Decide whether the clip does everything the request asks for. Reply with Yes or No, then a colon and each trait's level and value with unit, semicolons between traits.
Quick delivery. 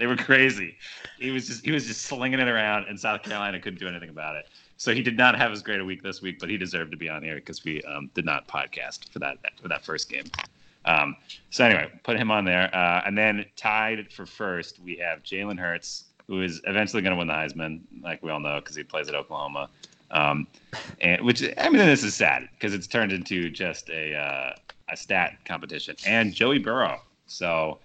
Yes: fast, 230 wpm